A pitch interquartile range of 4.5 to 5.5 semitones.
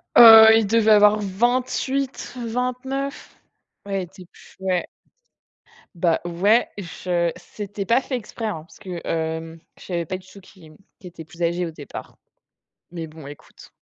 Yes: average, 4.8 semitones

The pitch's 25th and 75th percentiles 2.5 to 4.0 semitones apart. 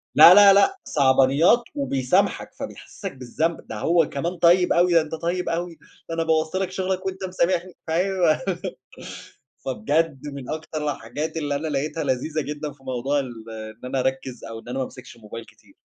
No: average, 4.8 semitones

